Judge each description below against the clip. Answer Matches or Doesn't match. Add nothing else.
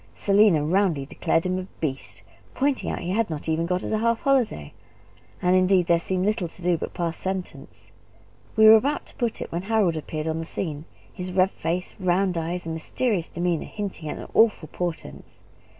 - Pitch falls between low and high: Matches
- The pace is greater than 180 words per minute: Matches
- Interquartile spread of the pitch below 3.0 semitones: Doesn't match